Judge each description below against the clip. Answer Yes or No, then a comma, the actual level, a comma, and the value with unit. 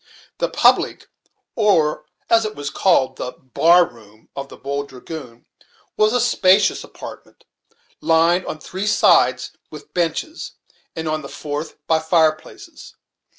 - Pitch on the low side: No, medium, 160 Hz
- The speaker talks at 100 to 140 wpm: Yes, slow, 135 wpm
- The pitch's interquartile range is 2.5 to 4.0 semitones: No, average, 5.3 semitones